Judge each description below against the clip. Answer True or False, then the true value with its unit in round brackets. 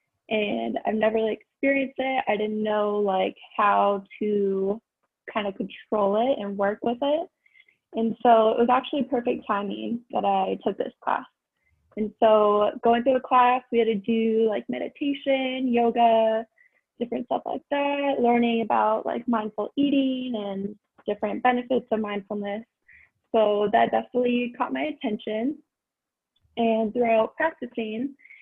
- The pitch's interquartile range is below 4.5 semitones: True (3.6 semitones)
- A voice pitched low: False (230 Hz)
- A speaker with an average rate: True (145 wpm)